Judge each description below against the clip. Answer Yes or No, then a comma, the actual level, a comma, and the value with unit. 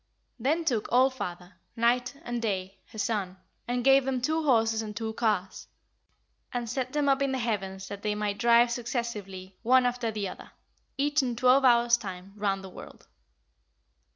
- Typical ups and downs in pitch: Yes, average, 3.8 semitones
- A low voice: No, high, 235 Hz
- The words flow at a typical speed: Yes, average, 175 wpm